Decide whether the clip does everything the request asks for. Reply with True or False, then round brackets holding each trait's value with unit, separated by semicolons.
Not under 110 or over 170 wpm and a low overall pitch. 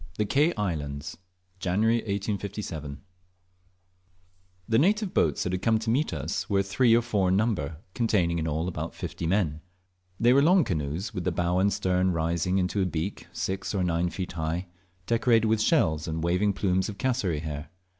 False (180 wpm; 95 Hz)